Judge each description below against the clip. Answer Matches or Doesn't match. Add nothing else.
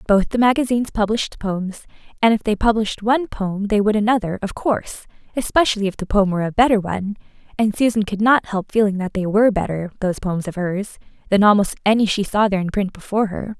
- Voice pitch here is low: Doesn't match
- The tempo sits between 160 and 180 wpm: Doesn't match